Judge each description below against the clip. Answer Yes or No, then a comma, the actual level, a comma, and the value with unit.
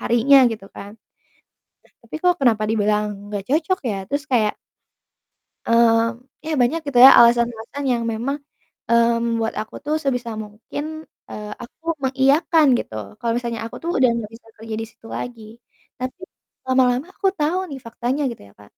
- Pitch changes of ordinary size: Yes, average, 3.4 semitones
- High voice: Yes, high, 235 Hz